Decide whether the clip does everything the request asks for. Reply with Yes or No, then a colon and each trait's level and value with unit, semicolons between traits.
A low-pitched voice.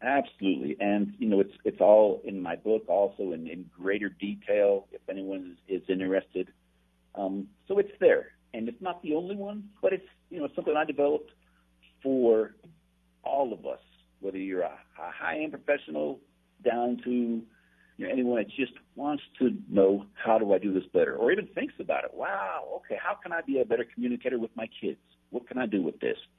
Yes: low, 105 Hz